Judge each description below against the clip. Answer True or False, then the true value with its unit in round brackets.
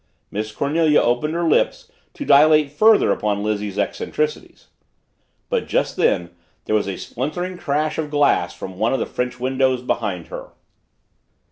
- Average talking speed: True (150 wpm)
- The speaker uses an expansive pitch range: True (6.2 semitones)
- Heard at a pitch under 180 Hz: True (135 Hz)